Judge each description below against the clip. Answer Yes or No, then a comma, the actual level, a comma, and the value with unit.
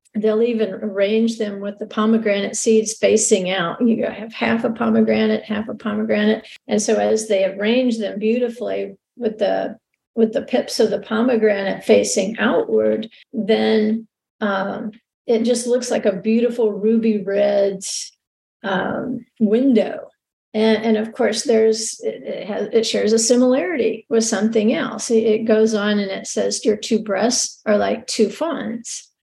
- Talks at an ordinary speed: Yes, average, 155 wpm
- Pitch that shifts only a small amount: Yes, narrow, 1.5 semitones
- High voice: Yes, high, 220 Hz